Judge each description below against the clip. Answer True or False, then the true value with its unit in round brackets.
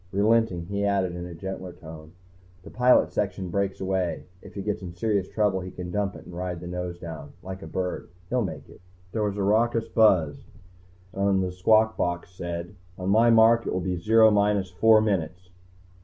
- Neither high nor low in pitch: False (95 Hz)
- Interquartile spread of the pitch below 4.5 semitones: True (3.0 semitones)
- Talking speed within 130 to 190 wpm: False (200 wpm)